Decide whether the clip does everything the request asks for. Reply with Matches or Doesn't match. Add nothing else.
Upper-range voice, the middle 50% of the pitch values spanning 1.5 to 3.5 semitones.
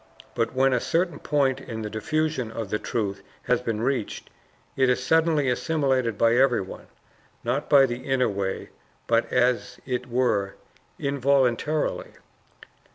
Doesn't match